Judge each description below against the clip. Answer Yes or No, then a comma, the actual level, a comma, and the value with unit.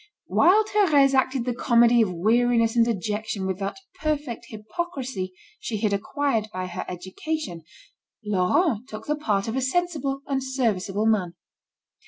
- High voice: Yes, high, 235 Hz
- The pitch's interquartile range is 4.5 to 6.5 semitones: Yes, average, 5.1 semitones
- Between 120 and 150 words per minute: Yes, average, 145 wpm